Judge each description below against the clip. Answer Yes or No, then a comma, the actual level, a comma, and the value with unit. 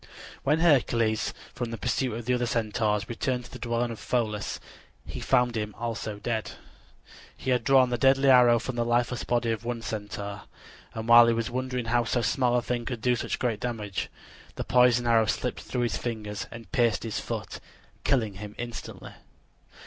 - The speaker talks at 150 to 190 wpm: Yes, average, 185 wpm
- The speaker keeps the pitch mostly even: Yes, narrow, 1.8 semitones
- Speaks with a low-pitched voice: Yes, low, 120 Hz